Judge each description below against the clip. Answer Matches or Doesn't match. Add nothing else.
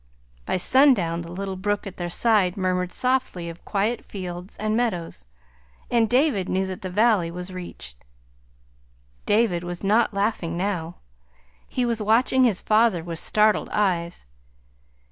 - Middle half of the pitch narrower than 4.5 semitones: Matches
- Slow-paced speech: Doesn't match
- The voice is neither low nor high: Doesn't match